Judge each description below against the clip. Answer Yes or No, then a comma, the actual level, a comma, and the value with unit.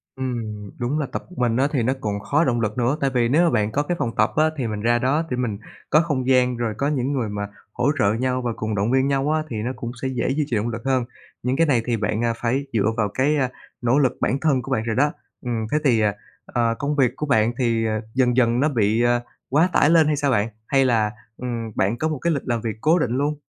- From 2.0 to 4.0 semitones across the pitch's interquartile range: Yes, average, 3.5 semitones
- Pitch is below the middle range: Yes, low, 125 Hz